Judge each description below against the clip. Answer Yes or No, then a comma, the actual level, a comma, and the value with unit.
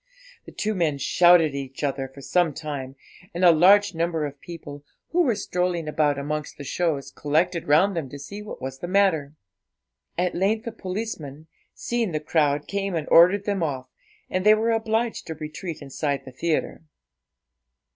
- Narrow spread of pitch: No, average, 5.0 semitones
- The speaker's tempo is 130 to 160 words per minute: No, average, 175 wpm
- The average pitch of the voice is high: No, medium, 165 Hz